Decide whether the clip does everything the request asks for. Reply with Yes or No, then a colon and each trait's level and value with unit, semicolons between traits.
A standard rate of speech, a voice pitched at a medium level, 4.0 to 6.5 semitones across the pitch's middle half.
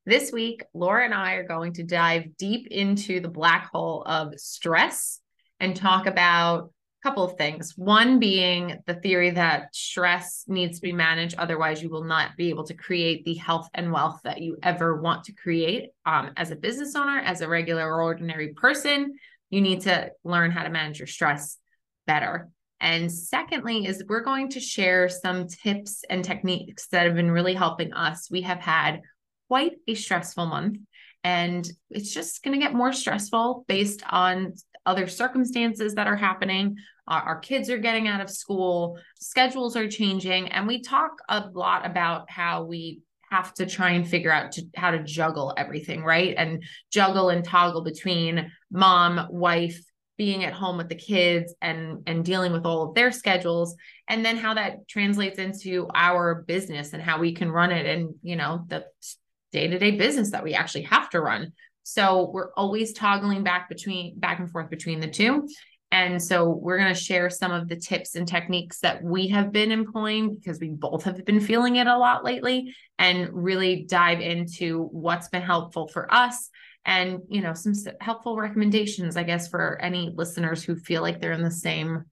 No: average, 185 wpm; medium, 180 Hz; average, 3.4 semitones